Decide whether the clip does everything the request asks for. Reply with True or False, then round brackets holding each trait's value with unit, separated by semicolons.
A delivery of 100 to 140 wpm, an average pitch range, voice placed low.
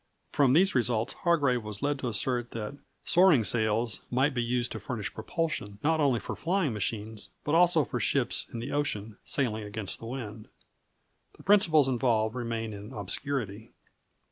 False (165 wpm; 4.6 semitones; 120 Hz)